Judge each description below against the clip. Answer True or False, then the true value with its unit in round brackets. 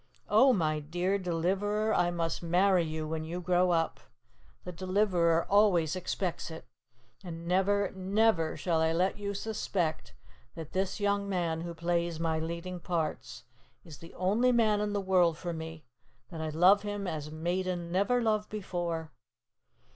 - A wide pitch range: False (3.3 semitones)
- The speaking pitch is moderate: True (180 Hz)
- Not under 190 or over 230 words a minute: False (155 wpm)